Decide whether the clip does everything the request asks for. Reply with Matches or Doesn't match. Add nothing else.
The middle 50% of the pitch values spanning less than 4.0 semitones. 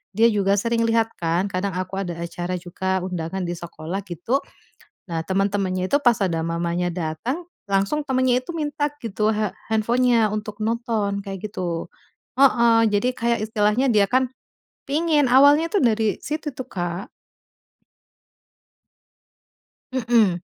Doesn't match